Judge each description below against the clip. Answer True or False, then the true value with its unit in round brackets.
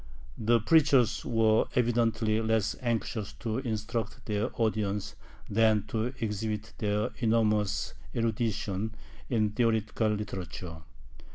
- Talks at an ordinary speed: False (100 wpm)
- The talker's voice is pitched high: False (110 Hz)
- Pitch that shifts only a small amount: True (1.5 semitones)